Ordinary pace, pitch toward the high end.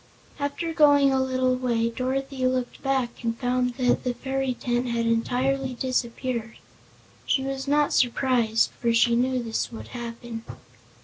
Yes: average, 145 wpm; very high, 255 Hz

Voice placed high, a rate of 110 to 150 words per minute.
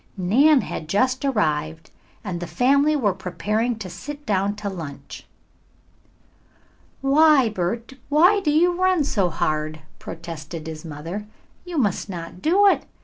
Yes: high, 210 Hz; average, 140 wpm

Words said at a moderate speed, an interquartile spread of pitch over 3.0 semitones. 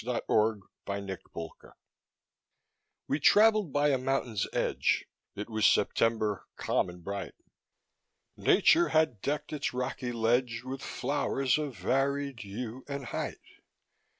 No: slow, 115 wpm; average, 4.6 semitones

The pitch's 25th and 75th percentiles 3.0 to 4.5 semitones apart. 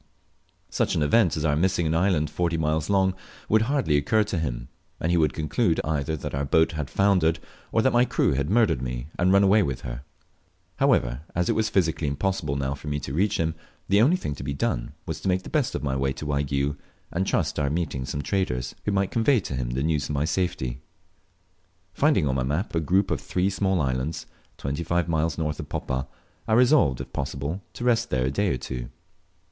No: wide, 5.5 semitones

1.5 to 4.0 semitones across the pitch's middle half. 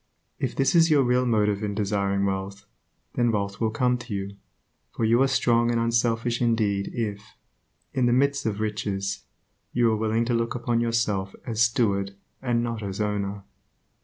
Yes: average, 3.0 semitones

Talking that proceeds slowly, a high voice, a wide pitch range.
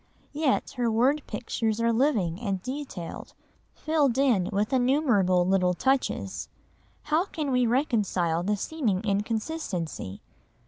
Yes: slow, 120 wpm; high, 230 Hz; wide, 6.2 semitones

